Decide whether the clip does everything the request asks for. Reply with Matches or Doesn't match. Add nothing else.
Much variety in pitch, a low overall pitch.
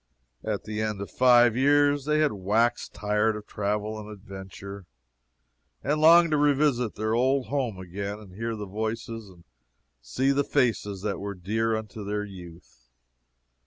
Doesn't match